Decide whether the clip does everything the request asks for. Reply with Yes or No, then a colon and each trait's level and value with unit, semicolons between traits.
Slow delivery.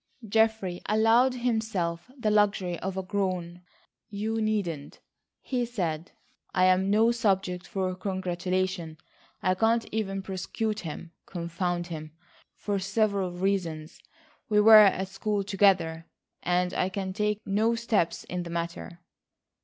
Yes: slow, 130 wpm